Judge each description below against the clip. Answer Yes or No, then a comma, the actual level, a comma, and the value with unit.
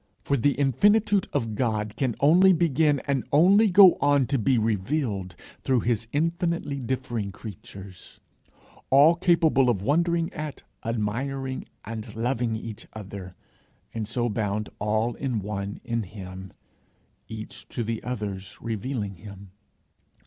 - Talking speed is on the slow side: Yes, slow, 130 wpm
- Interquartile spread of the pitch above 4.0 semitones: Yes, average, 5.3 semitones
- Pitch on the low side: Yes, low, 120 Hz